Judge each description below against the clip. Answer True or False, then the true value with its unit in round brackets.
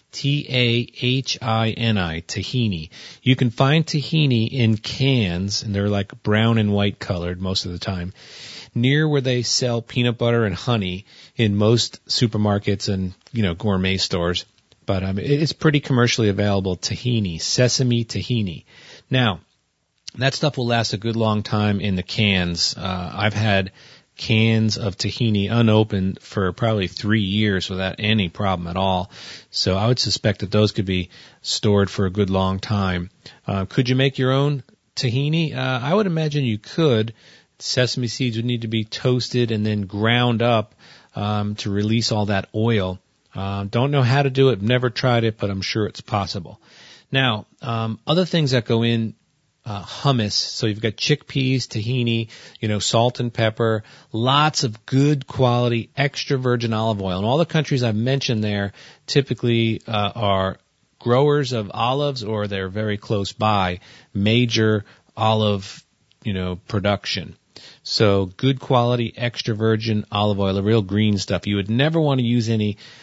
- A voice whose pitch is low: True (110 Hz)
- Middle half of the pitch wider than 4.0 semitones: False (3.7 semitones)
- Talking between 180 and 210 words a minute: False (165 wpm)